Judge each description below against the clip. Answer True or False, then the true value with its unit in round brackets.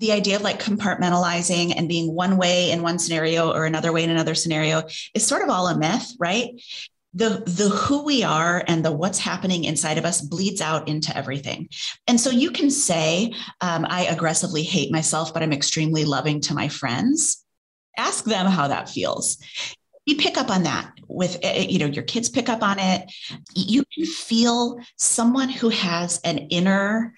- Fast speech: False (190 wpm)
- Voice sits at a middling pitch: True (180 Hz)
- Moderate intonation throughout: False (5.9 semitones)